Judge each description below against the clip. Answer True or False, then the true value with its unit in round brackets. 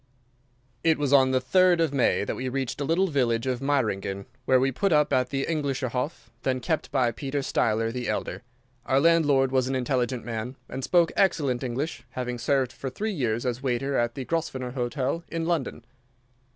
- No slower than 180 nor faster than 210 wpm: True (190 wpm)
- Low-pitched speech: True (130 Hz)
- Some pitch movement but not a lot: True (3.0 semitones)